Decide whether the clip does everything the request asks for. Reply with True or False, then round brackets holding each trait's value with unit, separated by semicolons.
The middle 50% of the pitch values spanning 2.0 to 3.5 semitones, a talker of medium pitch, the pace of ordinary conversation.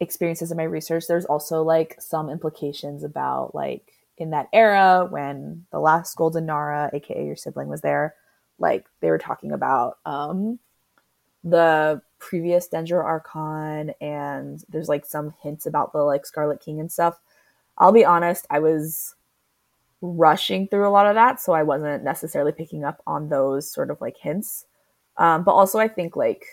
True (2.9 semitones; 160 Hz; 170 wpm)